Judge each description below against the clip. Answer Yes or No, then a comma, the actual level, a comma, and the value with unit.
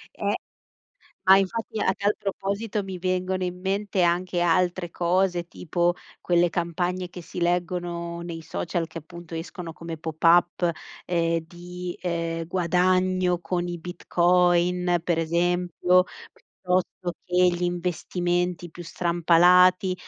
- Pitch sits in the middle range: Yes, medium, 175 Hz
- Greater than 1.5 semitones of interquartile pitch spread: No, narrow, 1.0 semitones